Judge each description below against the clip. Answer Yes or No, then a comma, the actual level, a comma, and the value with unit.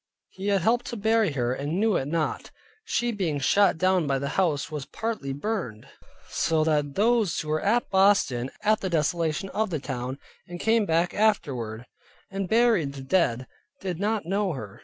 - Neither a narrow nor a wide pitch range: No, wide, 6.6 semitones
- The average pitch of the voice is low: No, medium, 175 Hz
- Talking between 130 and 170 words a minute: No, average, 180 wpm